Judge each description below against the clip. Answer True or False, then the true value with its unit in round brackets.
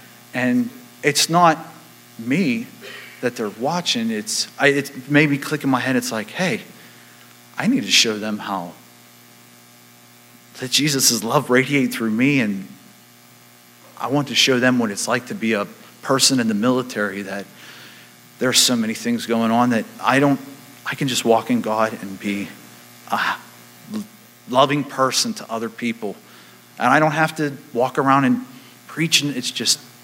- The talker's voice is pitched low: True (120 Hz)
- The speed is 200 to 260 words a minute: False (160 wpm)